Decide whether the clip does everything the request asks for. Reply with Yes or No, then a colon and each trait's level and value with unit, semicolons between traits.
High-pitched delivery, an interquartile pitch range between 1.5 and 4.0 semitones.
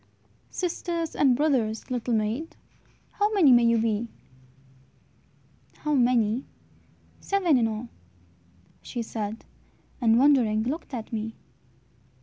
No: high, 240 Hz; average, 4.7 semitones